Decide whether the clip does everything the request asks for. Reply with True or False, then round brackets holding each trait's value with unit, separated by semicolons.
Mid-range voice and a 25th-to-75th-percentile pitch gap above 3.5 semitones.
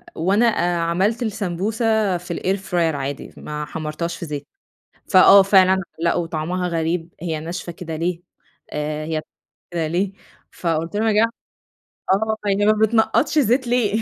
True (180 Hz; 4.0 semitones)